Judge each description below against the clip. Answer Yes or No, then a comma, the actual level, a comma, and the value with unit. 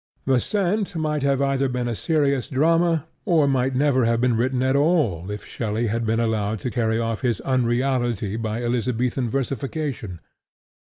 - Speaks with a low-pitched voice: Yes, low, 125 Hz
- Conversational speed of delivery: Yes, average, 170 wpm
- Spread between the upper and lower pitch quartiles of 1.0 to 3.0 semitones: No, average, 3.4 semitones